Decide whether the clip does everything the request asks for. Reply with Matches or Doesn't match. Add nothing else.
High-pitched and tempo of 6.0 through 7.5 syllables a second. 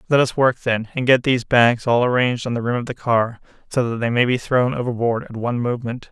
Doesn't match